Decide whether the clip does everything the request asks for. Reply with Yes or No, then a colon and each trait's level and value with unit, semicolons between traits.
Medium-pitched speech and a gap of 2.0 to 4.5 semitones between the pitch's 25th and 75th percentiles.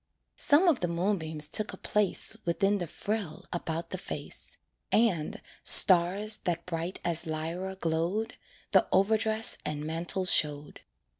Yes: medium, 175 Hz; average, 4.2 semitones